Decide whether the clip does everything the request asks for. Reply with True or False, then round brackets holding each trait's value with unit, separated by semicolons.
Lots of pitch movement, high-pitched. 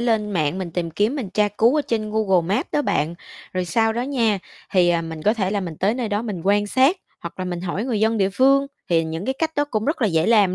False (4.6 semitones; 205 Hz)